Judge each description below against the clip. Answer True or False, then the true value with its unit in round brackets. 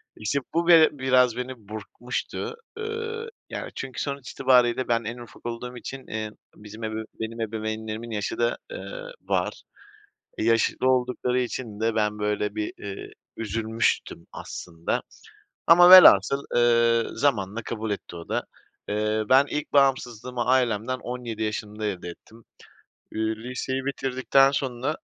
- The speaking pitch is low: True (120 Hz)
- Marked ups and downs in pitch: False (3.2 semitones)